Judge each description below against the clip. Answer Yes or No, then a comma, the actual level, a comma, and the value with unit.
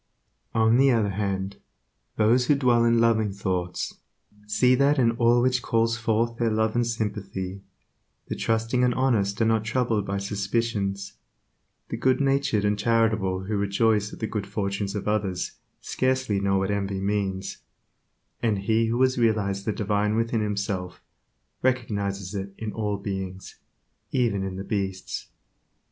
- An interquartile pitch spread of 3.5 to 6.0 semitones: No, average, 2.8 semitones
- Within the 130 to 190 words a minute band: Yes, average, 155 wpm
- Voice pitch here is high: No, low, 105 Hz